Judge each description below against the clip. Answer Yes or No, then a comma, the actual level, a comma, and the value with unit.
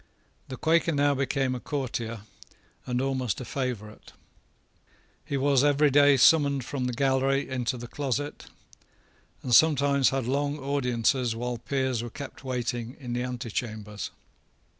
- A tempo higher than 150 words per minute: No, average, 140 wpm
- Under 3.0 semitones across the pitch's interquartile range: Yes, narrow, 2.5 semitones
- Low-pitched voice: Yes, low, 130 Hz